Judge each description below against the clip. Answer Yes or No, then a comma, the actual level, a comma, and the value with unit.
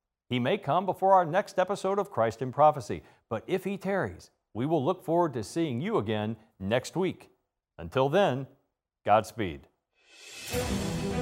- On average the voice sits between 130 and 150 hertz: Yes, low, 135 Hz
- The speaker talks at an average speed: Yes, average, 150 wpm